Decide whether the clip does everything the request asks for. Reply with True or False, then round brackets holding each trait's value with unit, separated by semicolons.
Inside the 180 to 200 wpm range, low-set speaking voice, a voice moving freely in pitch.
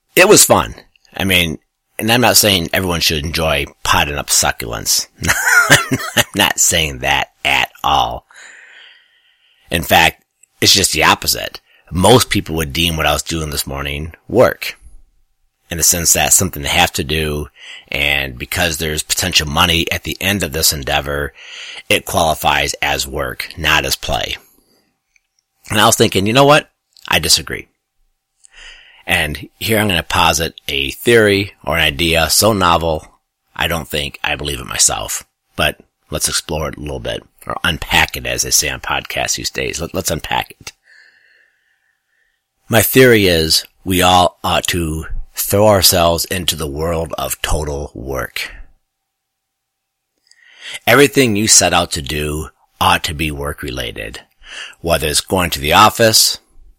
False (155 wpm; 85 Hz; 5.8 semitones)